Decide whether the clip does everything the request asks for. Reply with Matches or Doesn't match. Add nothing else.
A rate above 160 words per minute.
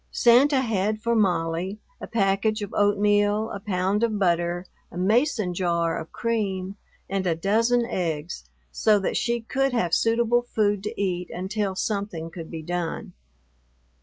Doesn't match